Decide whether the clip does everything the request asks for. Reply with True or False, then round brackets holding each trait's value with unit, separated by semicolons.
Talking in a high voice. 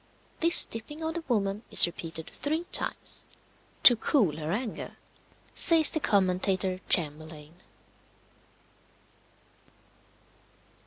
True (195 Hz)